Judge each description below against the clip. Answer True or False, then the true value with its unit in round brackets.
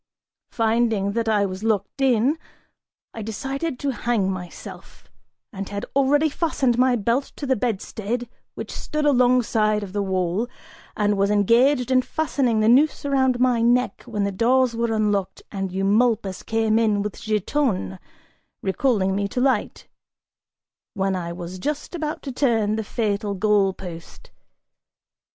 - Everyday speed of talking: True (145 wpm)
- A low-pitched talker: False (225 Hz)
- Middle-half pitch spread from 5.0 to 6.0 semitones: False (4.1 semitones)